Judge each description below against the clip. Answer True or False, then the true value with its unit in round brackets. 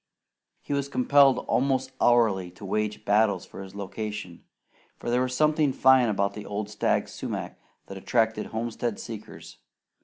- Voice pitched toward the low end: True (110 Hz)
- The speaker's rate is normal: True (150 wpm)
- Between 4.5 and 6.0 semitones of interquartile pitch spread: False (3.9 semitones)